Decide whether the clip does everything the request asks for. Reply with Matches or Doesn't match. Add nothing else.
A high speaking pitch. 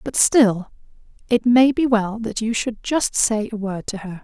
Matches